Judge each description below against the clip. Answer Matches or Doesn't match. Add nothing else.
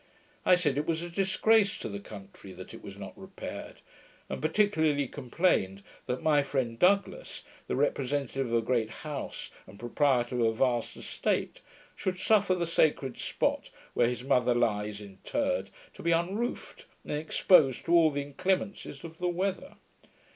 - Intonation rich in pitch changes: Matches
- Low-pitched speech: Doesn't match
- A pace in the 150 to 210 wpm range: Matches